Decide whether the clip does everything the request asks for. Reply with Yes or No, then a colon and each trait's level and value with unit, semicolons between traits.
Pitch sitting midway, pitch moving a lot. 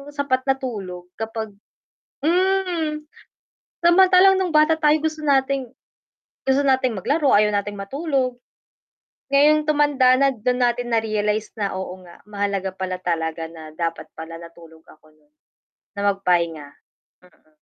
No: high, 225 Hz; wide, 8.1 semitones